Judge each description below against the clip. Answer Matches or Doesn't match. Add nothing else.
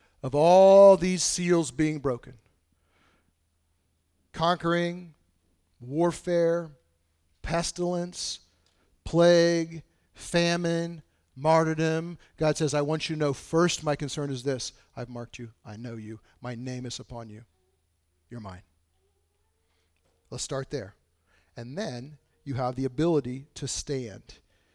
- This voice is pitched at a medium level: Doesn't match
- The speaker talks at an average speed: Doesn't match